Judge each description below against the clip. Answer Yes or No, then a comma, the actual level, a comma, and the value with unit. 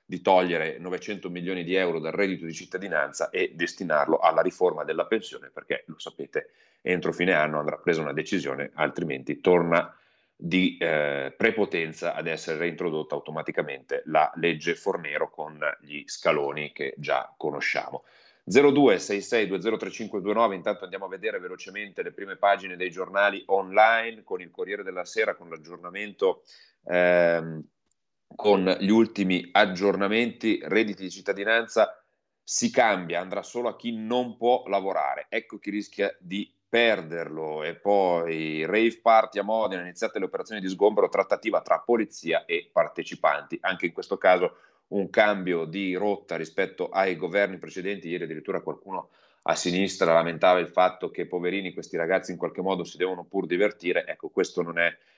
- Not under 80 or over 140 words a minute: No, average, 150 wpm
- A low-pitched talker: Yes, low, 100 Hz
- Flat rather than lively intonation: No, average, 4.7 semitones